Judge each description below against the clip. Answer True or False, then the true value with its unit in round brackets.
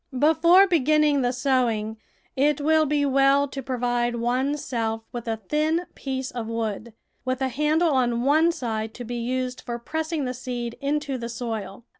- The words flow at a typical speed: True (170 wpm)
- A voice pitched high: True (255 Hz)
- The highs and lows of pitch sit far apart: False (3.8 semitones)